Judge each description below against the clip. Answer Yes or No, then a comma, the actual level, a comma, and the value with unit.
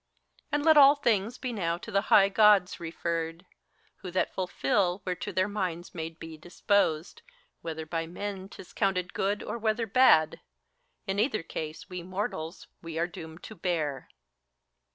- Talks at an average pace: Yes, average, 160 wpm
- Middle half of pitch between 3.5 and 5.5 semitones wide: Yes, average, 3.8 semitones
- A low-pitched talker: No, medium, 185 Hz